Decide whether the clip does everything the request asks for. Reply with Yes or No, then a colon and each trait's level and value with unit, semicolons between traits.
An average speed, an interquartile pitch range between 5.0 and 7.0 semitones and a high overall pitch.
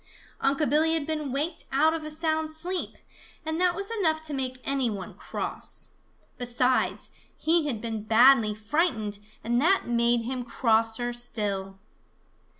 Yes: average, 150 wpm; average, 5.3 semitones; very high, 265 Hz